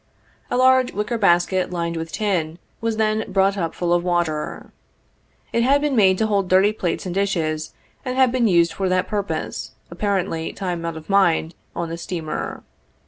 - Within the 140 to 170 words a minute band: No, average, 180 wpm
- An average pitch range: Yes, average, 4.1 semitones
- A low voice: No, medium, 185 Hz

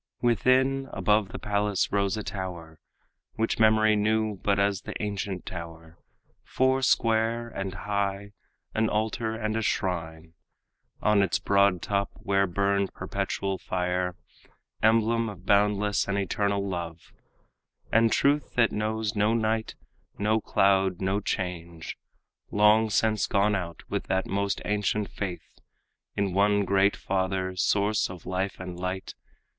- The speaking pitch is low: Yes, low, 100 Hz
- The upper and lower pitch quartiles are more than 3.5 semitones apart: No, narrow, 2.5 semitones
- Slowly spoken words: Yes, slow, 130 wpm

